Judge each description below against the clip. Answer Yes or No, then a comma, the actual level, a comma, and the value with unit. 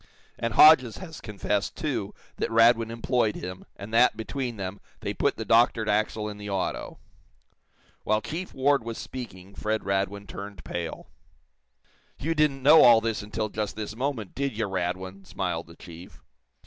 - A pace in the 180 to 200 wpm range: No, average, 160 wpm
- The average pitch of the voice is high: No, low, 110 Hz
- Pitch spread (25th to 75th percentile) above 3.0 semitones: Yes, average, 3.5 semitones